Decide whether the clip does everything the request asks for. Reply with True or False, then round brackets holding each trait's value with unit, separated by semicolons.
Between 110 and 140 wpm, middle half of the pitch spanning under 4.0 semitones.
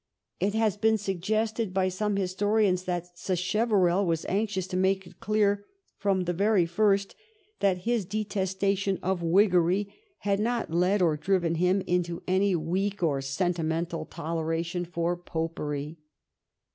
True (135 wpm; 2.8 semitones)